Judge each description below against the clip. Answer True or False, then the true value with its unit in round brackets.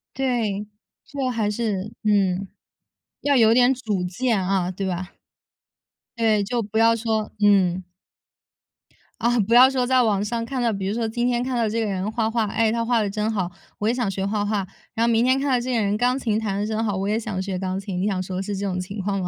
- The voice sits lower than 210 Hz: False (215 Hz)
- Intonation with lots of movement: False (3.2 semitones)